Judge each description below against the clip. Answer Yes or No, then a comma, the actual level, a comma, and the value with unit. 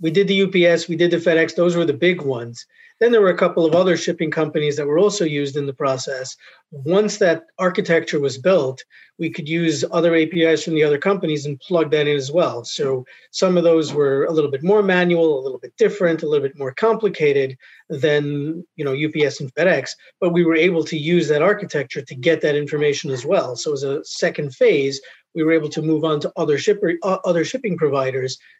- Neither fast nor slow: No, fast, 220 wpm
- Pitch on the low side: No, medium, 160 Hz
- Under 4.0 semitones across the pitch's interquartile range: Yes, average, 3.5 semitones